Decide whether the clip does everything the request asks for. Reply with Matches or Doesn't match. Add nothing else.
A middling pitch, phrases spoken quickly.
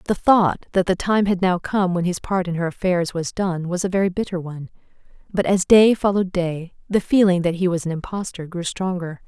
Matches